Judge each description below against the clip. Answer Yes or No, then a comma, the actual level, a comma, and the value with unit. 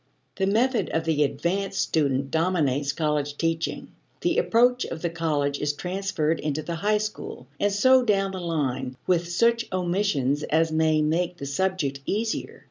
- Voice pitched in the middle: Yes, medium, 165 Hz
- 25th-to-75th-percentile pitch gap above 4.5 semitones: Yes, average, 4.9 semitones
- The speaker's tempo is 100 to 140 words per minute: No, average, 160 wpm